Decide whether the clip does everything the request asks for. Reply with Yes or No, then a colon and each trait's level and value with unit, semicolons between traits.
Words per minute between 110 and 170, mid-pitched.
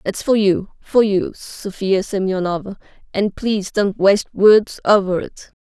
No: average, 150 wpm; high, 200 Hz